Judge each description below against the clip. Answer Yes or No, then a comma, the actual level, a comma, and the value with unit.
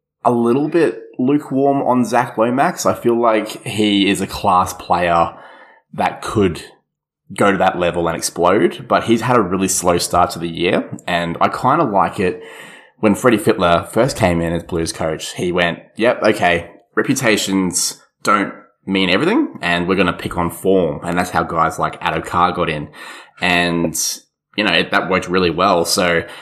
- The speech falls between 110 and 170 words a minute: No, average, 180 wpm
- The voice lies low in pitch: Yes, very low, 90 Hz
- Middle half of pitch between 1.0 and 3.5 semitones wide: No, average, 4.8 semitones